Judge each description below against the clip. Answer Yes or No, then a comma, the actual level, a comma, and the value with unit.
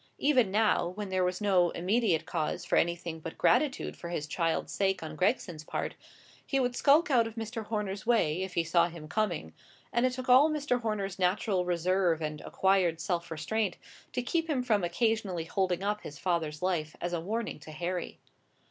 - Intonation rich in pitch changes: No, average, 4.8 semitones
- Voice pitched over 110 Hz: Yes, high, 190 Hz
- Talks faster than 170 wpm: Yes, average, 190 wpm